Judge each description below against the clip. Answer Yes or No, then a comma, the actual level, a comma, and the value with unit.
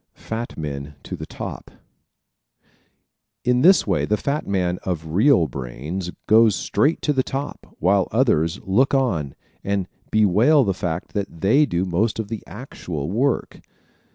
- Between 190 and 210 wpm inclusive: No, average, 155 wpm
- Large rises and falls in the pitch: Yes, wide, 6.3 semitones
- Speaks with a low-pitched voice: Yes, low, 100 Hz